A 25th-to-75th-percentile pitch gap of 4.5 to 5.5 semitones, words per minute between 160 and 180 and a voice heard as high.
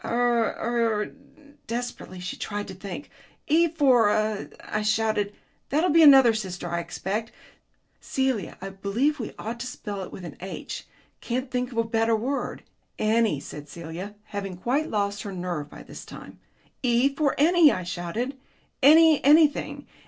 Yes: average, 5.2 semitones; average, 165 wpm; high, 225 Hz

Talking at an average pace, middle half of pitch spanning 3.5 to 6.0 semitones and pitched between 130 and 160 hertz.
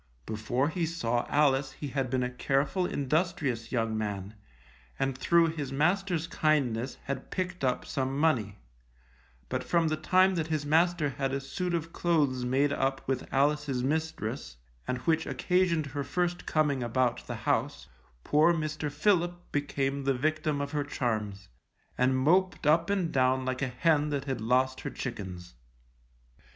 Yes: average, 160 wpm; average, 3.9 semitones; medium, 140 Hz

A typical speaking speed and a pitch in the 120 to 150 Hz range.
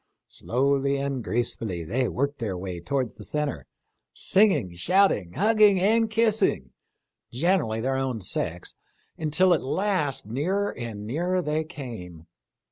No: slow, 125 wpm; medium, 140 Hz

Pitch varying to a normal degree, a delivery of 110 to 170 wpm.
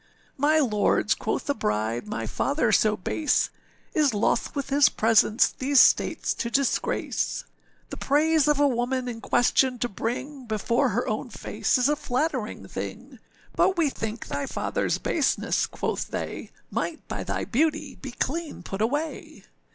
Yes: average, 4.6 semitones; average, 160 wpm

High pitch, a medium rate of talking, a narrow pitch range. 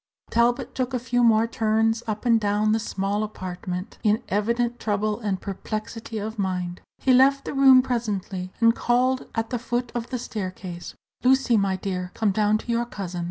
No: high, 220 Hz; average, 180 wpm; average, 3.3 semitones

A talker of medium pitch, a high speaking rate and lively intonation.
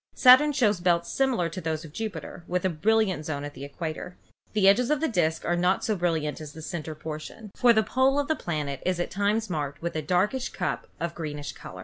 Yes: medium, 175 Hz; fast, 230 wpm; wide, 5.7 semitones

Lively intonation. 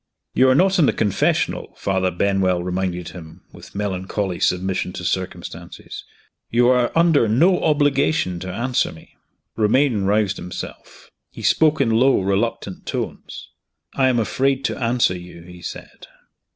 Yes: wide, 6.0 semitones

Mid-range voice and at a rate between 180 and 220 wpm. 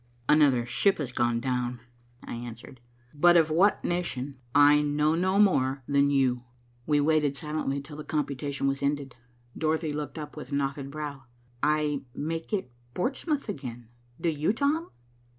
No: medium, 145 Hz; average, 150 wpm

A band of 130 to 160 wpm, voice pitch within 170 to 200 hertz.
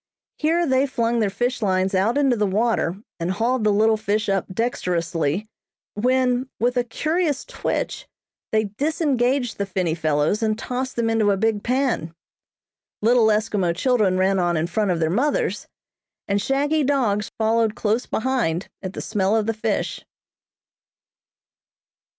No: average, 150 wpm; high, 220 Hz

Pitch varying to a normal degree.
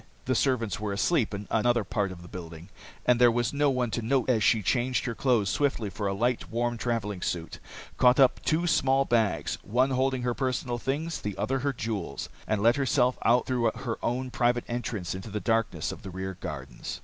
Yes: average, 3.8 semitones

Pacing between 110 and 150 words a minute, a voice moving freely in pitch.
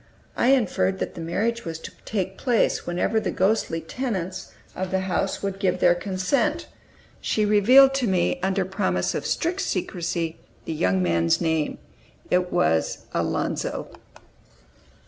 No: average, 145 wpm; average, 4.3 semitones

